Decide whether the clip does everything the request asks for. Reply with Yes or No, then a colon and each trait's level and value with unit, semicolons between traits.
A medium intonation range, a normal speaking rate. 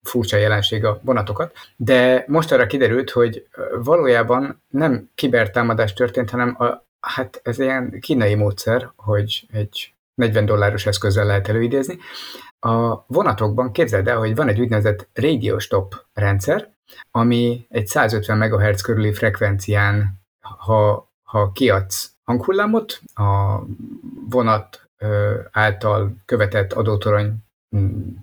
Yes: average, 3.1 semitones; average, 115 wpm